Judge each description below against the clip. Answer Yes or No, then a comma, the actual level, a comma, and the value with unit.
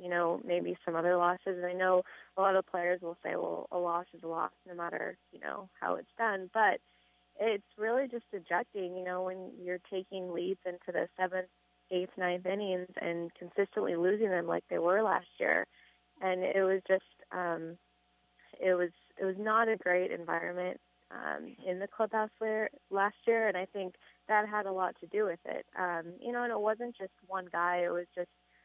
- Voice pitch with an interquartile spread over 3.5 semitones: No, narrow, 2.4 semitones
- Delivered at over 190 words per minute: Yes, average, 200 wpm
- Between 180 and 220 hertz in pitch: Yes, medium, 185 Hz